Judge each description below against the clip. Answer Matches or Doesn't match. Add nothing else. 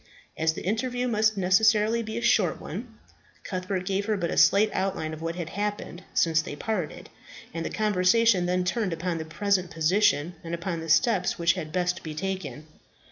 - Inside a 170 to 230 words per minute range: Matches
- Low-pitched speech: Doesn't match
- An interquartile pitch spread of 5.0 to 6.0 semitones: Doesn't match